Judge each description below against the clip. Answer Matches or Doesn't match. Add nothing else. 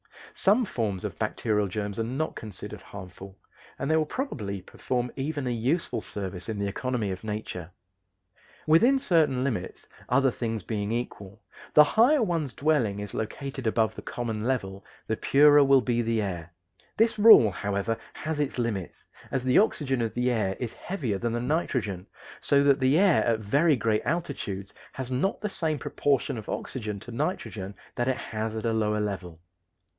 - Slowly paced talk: Doesn't match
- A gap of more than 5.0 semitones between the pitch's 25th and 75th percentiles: Matches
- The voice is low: Matches